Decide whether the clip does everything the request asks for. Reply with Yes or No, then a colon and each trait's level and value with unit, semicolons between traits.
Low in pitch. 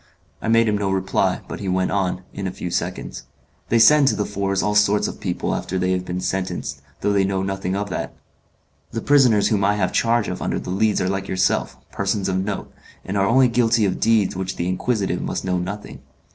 Yes: low, 100 Hz